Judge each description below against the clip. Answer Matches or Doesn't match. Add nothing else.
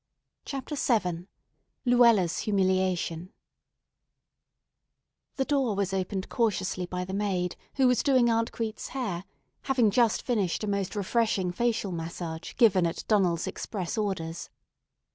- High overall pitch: Matches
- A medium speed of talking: Doesn't match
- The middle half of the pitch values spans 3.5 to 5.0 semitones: Matches